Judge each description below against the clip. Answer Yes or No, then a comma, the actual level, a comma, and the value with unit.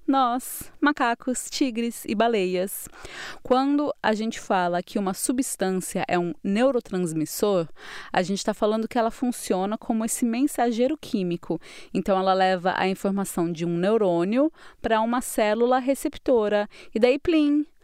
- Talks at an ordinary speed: Yes, average, 140 wpm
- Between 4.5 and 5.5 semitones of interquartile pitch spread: Yes, average, 5.1 semitones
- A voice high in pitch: Yes, high, 225 Hz